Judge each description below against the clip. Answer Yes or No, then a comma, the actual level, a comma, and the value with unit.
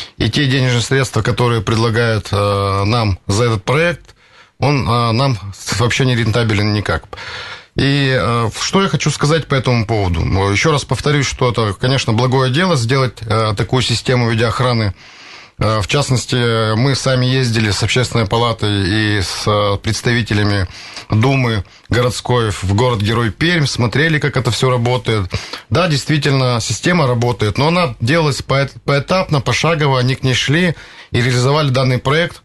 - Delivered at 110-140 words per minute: Yes, average, 135 wpm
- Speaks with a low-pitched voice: Yes, low, 120 Hz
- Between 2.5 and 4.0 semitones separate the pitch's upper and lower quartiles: Yes, average, 3.3 semitones